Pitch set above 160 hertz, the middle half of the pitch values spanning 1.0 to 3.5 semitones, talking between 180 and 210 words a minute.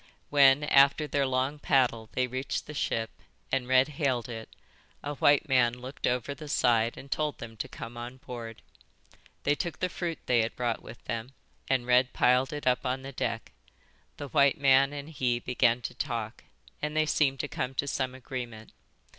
No: low, 130 Hz; average, 2.8 semitones; average, 190 wpm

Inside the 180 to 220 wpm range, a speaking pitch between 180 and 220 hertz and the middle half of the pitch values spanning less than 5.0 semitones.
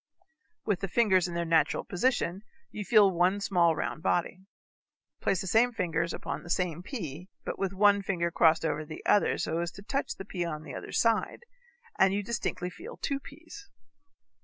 Yes: average, 185 wpm; medium, 185 Hz; average, 3.5 semitones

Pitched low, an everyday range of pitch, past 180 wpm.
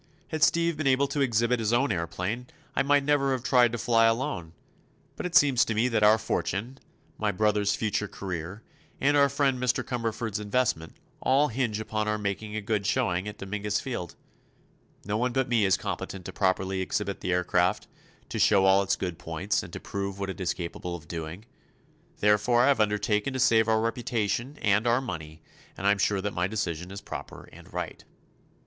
Yes: low, 105 Hz; average, 4.2 semitones; average, 195 wpm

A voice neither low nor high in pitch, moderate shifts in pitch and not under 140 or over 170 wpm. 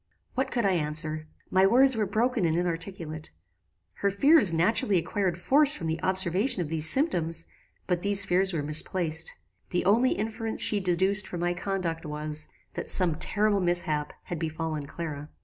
Yes: medium, 175 Hz; average, 3.8 semitones; average, 165 wpm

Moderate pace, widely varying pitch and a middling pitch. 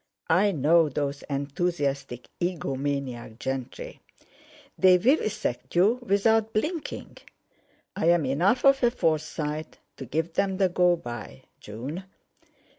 No: slow, 110 wpm; wide, 5.9 semitones; medium, 165 Hz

